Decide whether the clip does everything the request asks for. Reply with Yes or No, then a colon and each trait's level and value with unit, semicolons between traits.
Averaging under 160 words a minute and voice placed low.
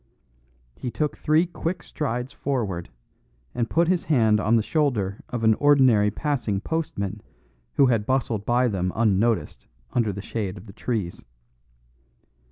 Yes: average, 145 wpm; low, 115 Hz